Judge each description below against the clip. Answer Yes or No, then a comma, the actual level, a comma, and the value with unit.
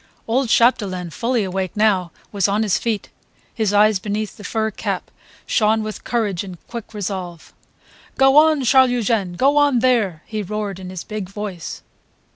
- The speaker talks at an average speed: Yes, average, 165 wpm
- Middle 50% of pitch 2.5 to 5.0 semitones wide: Yes, average, 3.5 semitones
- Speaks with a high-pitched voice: Yes, high, 215 Hz